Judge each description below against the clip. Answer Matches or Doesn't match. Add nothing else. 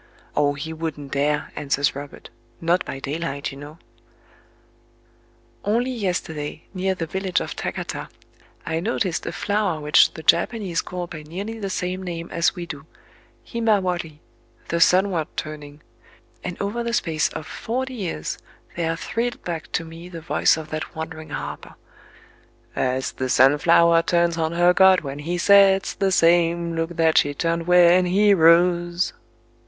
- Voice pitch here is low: Doesn't match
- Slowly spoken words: Doesn't match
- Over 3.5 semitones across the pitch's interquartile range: Doesn't match